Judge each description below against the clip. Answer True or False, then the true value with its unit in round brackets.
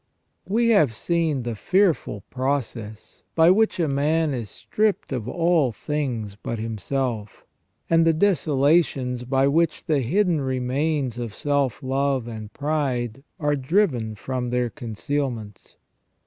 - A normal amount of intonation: True (4.9 semitones)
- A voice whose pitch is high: False (135 Hz)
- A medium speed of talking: False (130 wpm)